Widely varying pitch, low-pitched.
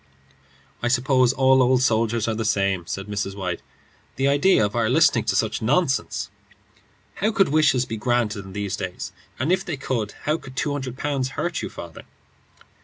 No: average, 4.6 semitones; low, 125 Hz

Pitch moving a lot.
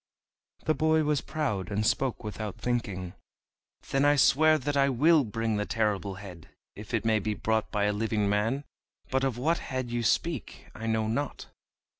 No: average, 4.9 semitones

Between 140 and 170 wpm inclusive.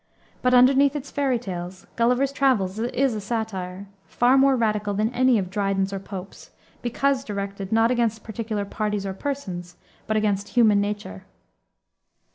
Yes: average, 150 wpm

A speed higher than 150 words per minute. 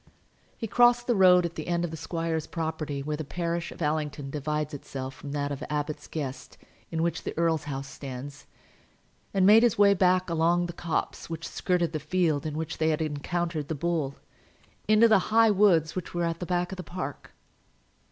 Yes: average, 200 wpm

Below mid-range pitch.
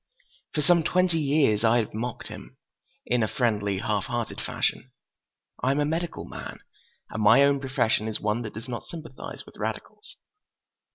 Yes: low, 125 Hz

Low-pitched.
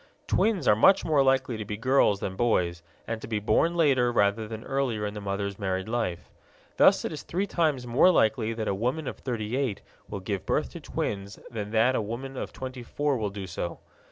Yes: low, 115 Hz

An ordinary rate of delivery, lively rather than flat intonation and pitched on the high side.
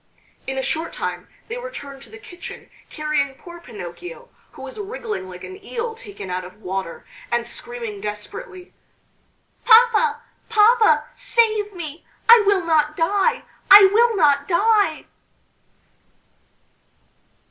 No: slow, 125 wpm; wide, 8.7 semitones; very high, 360 Hz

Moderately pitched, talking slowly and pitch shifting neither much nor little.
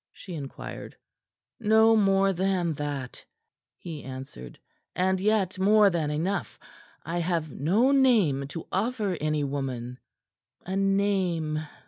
Yes: medium, 180 Hz; slow, 115 wpm; average, 5.0 semitones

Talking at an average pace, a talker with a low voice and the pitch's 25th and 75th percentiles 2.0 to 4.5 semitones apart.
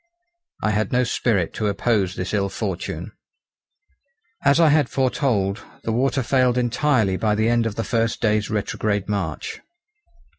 Yes: average, 150 wpm; low, 110 Hz; average, 3.6 semitones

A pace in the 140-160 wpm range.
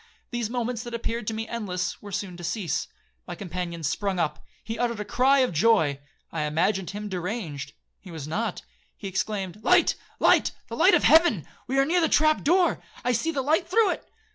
No: average, 190 wpm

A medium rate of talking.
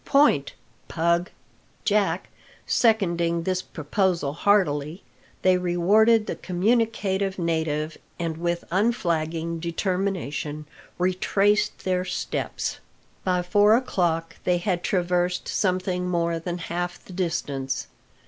No: slow, 100 wpm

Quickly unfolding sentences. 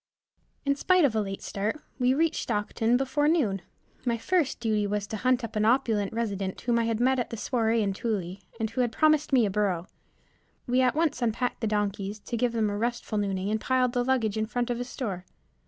Yes: fast, 220 wpm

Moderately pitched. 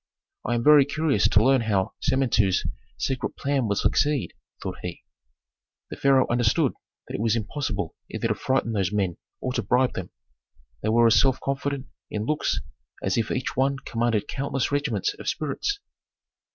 No: low, 125 Hz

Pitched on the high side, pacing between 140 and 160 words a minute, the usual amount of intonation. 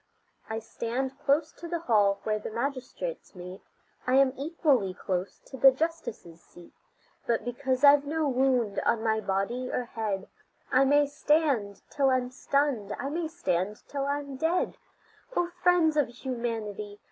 Yes: very high, 260 Hz; average, 155 wpm; average, 5.0 semitones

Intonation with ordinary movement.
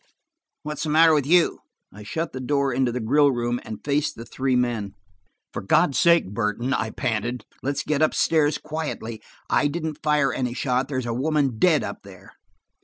Yes: average, 4.1 semitones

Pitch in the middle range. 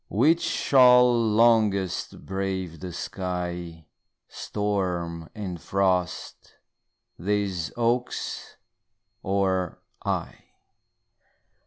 No: very low, 95 Hz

